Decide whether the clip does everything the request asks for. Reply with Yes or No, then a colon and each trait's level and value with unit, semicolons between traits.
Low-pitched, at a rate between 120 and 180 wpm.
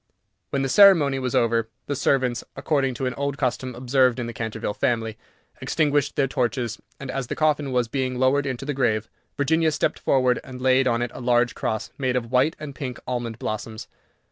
No: low, 130 Hz; average, 195 wpm